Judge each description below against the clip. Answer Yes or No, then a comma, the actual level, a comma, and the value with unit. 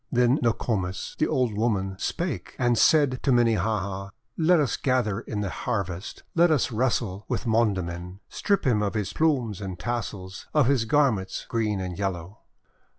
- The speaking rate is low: No, average, 155 wpm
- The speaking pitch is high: No, low, 110 Hz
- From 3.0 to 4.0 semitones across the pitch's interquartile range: No, average, 4.8 semitones